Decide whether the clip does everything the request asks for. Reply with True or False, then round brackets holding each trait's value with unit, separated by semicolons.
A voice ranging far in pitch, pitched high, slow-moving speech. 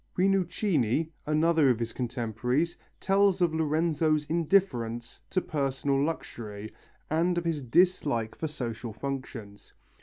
False (6.0 semitones; 150 Hz; 120 wpm)